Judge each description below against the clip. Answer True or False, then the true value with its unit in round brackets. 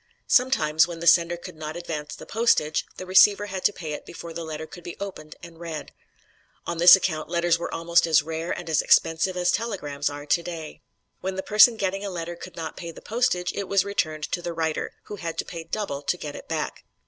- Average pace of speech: False (225 wpm)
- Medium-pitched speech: True (170 Hz)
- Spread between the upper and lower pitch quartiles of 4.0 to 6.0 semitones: False (2.8 semitones)